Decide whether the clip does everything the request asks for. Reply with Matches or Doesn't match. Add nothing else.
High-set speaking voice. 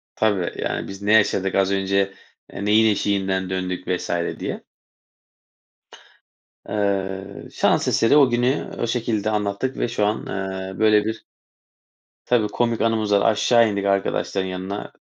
Doesn't match